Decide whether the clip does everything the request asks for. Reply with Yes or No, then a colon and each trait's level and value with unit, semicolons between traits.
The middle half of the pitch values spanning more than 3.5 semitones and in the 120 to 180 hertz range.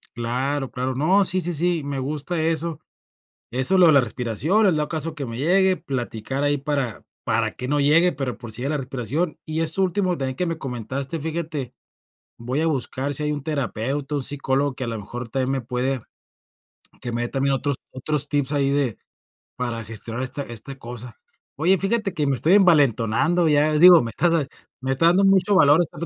Yes: average, 4.3 semitones; medium, 140 Hz